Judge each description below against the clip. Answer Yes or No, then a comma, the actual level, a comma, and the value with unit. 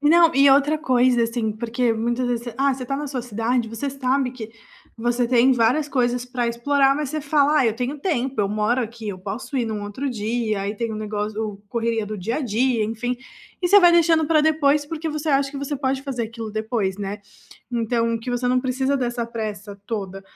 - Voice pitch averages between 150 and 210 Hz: No, high, 245 Hz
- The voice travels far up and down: No, average, 3.6 semitones